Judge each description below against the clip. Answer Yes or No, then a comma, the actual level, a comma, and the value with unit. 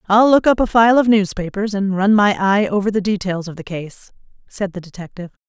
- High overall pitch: Yes, high, 200 Hz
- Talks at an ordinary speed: No, fast, 220 wpm